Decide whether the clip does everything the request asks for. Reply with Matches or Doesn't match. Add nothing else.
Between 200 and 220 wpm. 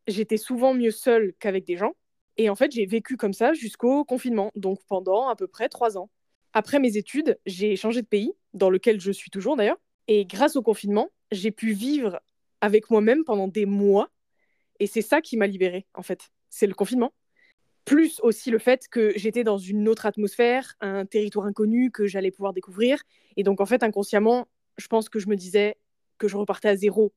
Matches